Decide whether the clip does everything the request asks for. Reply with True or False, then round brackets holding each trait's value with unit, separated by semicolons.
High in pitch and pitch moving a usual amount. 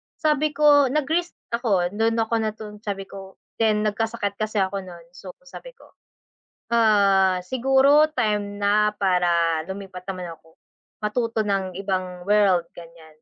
True (205 Hz; 3.6 semitones)